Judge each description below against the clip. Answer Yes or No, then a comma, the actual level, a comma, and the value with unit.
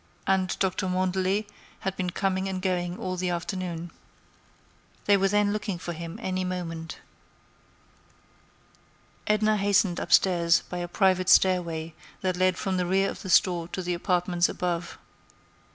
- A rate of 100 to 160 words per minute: Yes, average, 145 wpm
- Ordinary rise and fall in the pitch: No, narrow, 1.6 semitones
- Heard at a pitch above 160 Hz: Yes, medium, 185 Hz